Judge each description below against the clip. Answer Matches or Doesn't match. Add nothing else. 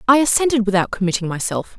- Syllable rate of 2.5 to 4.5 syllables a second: Doesn't match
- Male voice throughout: Doesn't match